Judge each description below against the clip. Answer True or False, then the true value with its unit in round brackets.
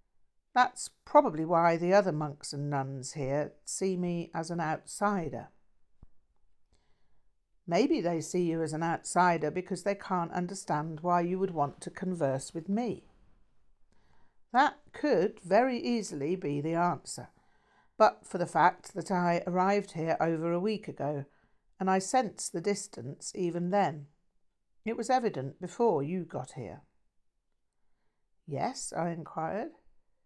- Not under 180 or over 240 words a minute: False (135 wpm)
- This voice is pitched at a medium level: True (170 Hz)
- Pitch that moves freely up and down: False (4.5 semitones)